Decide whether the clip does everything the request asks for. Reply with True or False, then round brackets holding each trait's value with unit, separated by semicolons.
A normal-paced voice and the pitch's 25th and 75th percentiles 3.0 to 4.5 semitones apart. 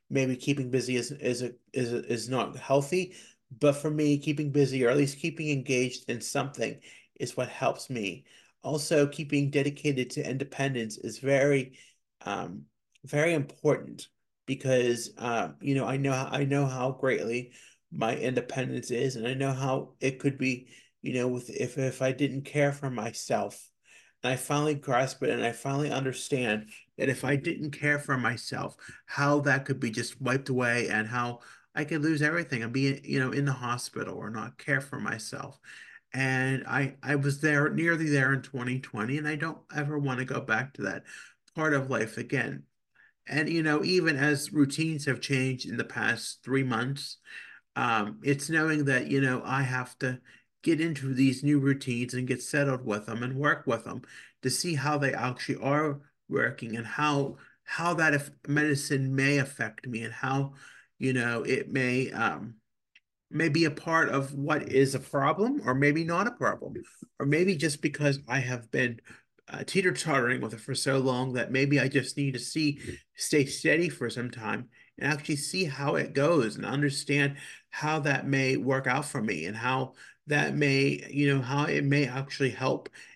False (185 wpm; 2.4 semitones)